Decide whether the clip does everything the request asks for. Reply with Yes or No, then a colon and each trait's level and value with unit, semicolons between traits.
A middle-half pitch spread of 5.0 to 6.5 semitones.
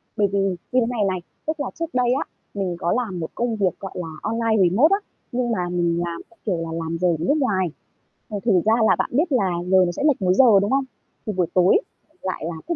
Yes: wide, 5.4 semitones